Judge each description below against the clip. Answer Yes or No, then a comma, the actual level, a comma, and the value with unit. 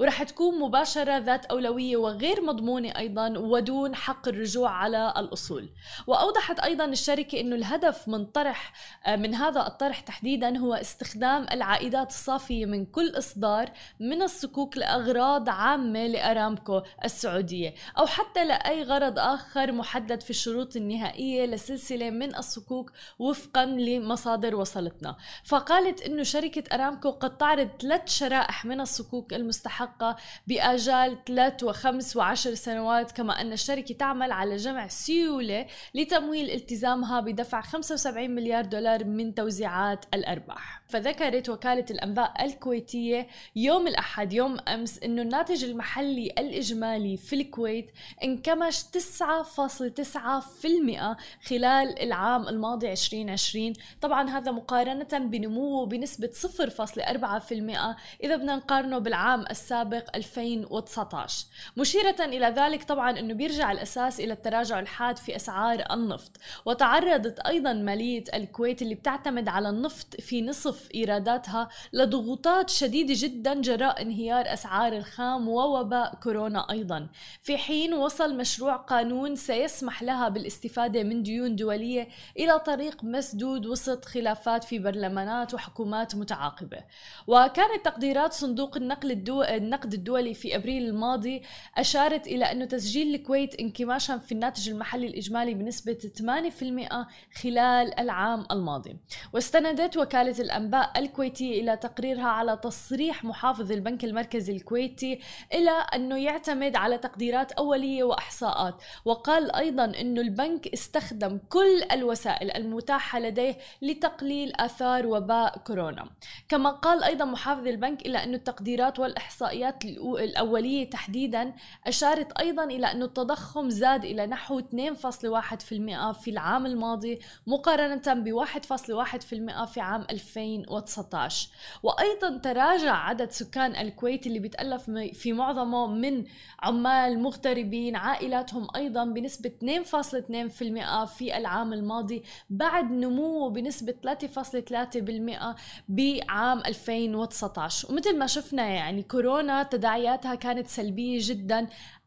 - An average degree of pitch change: Yes, average, 3.2 semitones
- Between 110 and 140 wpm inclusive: Yes, average, 115 wpm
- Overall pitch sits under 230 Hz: No, high, 245 Hz